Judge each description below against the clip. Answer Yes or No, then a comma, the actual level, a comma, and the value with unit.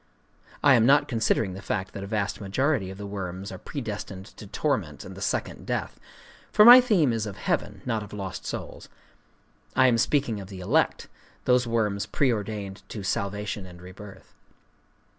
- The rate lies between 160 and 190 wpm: Yes, average, 170 wpm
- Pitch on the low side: Yes, low, 105 Hz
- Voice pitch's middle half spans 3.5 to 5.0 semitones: Yes, average, 4.0 semitones